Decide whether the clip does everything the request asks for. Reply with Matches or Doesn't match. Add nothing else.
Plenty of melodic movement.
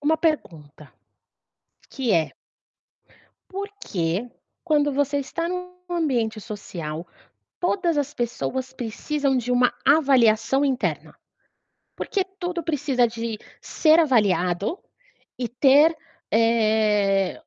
Matches